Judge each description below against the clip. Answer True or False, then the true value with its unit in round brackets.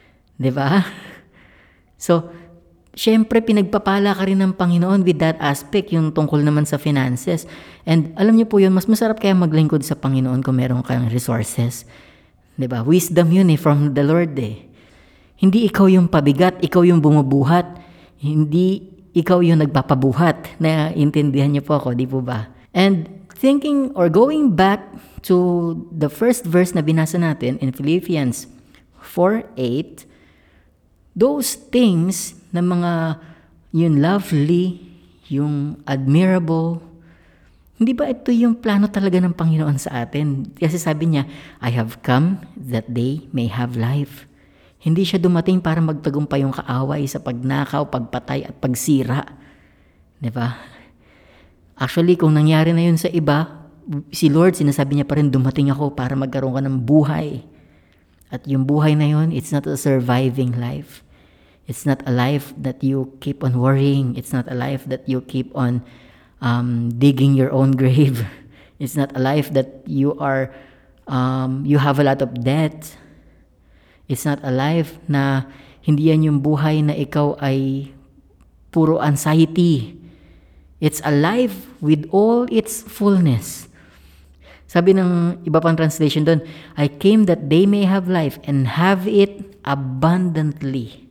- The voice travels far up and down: False (4.7 semitones)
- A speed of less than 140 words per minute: False (145 wpm)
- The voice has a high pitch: False (150 Hz)